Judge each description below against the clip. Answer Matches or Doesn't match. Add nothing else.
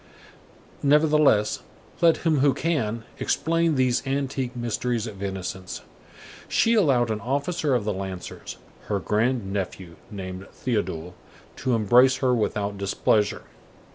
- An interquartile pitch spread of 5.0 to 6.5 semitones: Matches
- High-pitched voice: Doesn't match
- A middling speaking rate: Doesn't match